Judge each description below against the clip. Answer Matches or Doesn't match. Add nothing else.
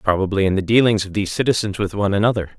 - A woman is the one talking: Doesn't match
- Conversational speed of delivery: Doesn't match